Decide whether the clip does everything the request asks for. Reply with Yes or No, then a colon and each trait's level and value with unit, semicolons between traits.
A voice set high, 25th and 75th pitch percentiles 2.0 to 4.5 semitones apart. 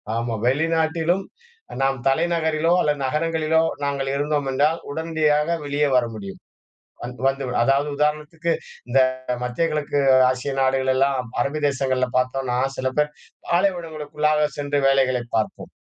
No: medium, 145 Hz; average, 2.9 semitones